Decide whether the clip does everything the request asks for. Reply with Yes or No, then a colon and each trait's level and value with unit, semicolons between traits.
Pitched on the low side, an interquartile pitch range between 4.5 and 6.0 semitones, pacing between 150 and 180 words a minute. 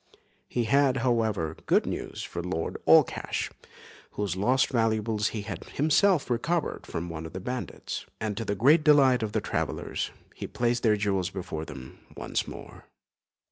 Yes: low, 110 Hz; average, 5.2 semitones; average, 160 wpm